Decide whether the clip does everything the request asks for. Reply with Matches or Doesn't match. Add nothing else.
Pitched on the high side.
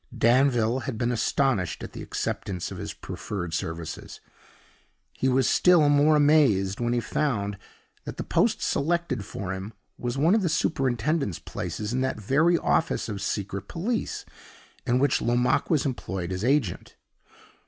Doesn't match